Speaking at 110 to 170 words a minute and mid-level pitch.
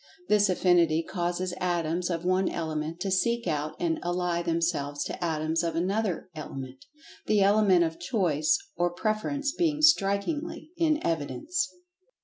Yes: average, 140 wpm; medium, 175 Hz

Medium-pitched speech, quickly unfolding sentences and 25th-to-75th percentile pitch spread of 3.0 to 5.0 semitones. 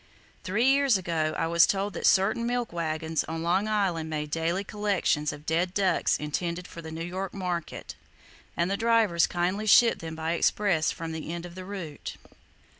No: medium, 175 Hz; average, 185 wpm; average, 3.6 semitones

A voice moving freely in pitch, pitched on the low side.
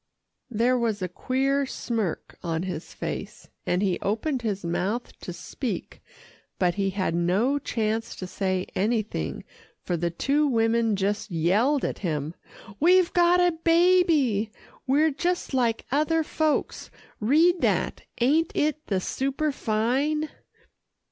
No: wide, 7.5 semitones; high, 235 Hz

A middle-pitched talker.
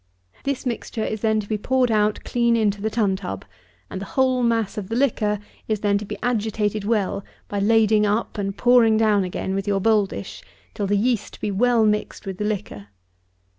No: high, 215 Hz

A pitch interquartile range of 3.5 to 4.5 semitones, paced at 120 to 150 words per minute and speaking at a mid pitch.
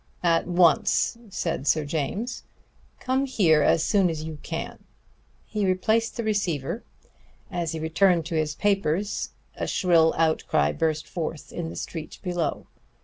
Yes: average, 3.8 semitones; average, 145 wpm; medium, 170 Hz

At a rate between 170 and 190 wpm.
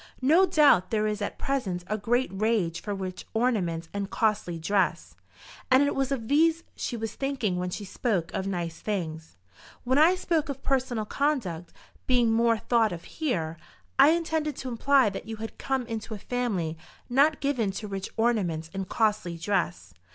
Yes: average, 175 wpm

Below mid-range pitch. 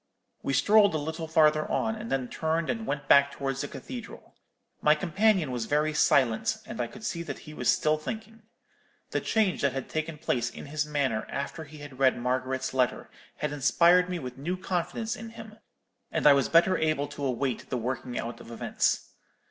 No: medium, 150 Hz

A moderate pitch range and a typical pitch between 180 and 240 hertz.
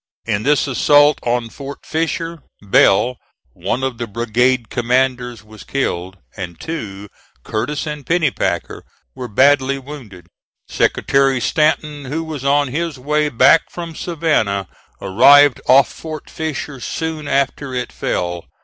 No: average, 4.2 semitones; low, 135 Hz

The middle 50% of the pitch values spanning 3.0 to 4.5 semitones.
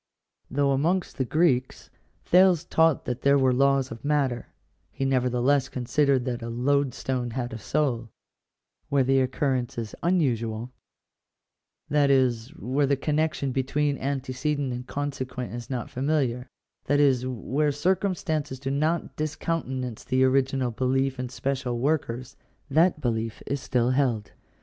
No: narrow, 2.5 semitones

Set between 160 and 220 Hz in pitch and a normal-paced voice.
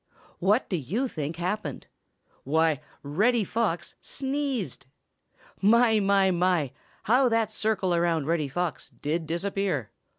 No: medium, 185 Hz; slow, 120 wpm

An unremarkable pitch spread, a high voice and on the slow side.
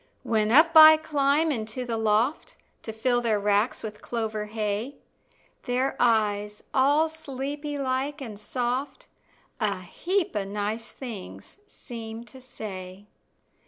Yes: average, 4.7 semitones; high, 235 Hz; slow, 125 wpm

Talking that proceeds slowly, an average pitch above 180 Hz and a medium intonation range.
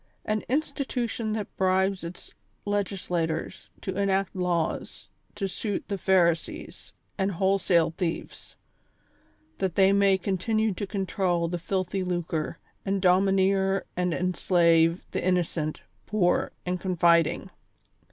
No: slow, 115 wpm; high, 190 Hz; narrow, 2.2 semitones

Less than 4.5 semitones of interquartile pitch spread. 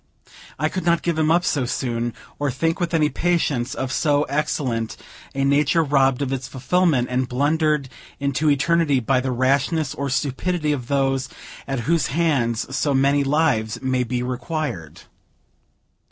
Yes: average, 3.4 semitones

